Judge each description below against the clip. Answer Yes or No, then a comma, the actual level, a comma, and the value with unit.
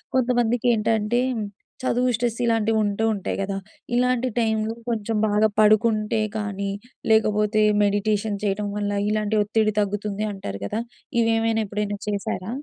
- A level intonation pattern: Yes, narrow, 1.6 semitones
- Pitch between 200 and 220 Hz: Yes, high, 215 Hz